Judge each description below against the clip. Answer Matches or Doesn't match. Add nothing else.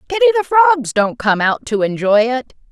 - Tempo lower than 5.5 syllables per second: Doesn't match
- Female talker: Matches